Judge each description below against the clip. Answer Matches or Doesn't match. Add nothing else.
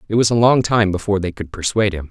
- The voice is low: Matches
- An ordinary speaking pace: Doesn't match